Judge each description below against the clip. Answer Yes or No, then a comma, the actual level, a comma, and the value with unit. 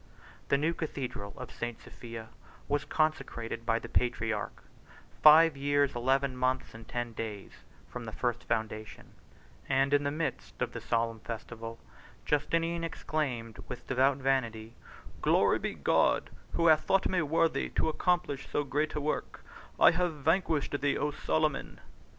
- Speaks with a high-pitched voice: No, low, 135 Hz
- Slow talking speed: No, average, 150 wpm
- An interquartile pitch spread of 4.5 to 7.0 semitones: Yes, average, 4.9 semitones